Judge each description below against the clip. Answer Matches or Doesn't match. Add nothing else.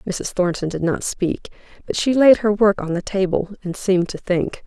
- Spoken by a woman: Matches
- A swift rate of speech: Matches